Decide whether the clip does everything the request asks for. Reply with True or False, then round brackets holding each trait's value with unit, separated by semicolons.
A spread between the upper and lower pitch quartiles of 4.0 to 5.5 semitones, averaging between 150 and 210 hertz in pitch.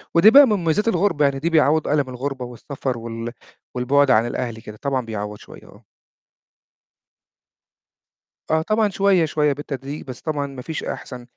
False (4.4 semitones; 140 Hz)